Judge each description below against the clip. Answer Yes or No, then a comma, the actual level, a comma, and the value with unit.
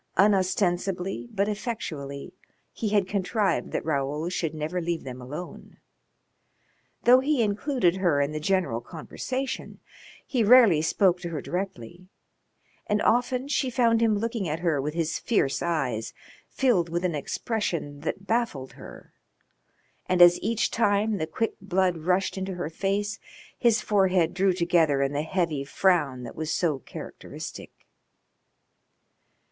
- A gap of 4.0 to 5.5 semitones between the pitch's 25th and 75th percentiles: Yes, average, 4.9 semitones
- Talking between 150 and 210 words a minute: No, average, 140 wpm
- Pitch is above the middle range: No, medium, 180 Hz